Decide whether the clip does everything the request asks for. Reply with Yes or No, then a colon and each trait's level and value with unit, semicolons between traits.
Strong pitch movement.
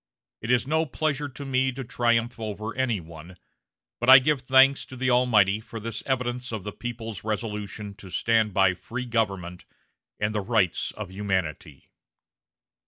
No: average, 4.0 semitones